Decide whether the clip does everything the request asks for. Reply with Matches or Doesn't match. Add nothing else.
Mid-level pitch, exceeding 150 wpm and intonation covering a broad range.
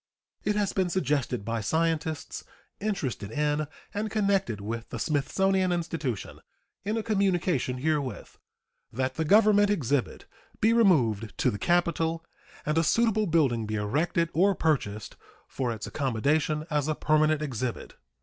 Doesn't match